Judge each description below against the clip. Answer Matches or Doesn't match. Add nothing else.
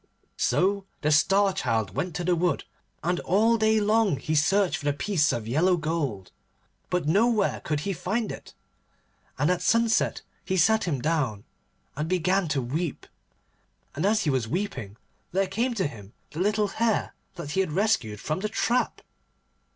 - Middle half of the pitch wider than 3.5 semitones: Matches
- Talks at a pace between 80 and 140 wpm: Doesn't match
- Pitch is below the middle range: Doesn't match